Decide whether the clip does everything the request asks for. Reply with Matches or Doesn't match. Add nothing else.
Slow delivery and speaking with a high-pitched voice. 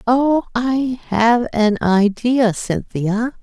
Matches